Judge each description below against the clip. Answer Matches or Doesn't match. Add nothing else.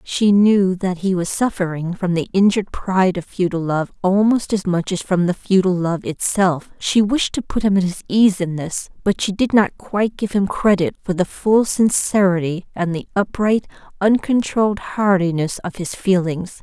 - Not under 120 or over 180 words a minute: Doesn't match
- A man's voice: Doesn't match